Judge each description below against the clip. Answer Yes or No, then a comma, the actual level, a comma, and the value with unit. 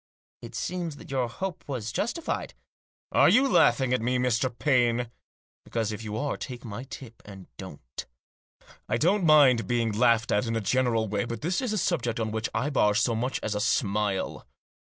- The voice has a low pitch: Yes, low, 120 Hz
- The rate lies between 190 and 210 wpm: Yes, average, 200 wpm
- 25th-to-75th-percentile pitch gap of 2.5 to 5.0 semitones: Yes, average, 3.7 semitones